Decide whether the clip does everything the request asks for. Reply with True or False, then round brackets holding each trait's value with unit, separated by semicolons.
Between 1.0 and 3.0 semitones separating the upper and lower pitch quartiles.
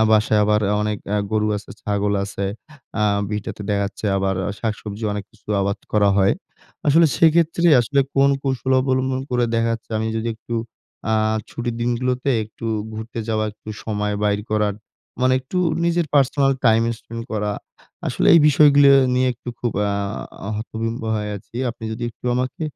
False (3.6 semitones)